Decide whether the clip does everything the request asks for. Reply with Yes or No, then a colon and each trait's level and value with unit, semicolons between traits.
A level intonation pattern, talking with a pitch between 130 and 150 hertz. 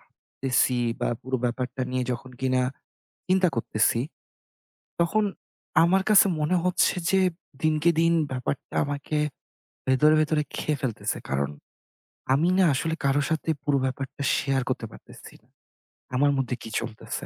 No: average, 3.9 semitones; medium, 140 Hz